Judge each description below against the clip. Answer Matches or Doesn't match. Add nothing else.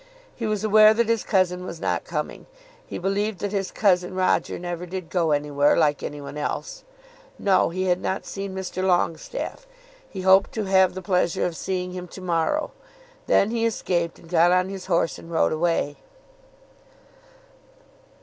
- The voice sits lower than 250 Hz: Matches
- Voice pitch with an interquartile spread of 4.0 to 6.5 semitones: Doesn't match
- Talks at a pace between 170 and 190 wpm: Matches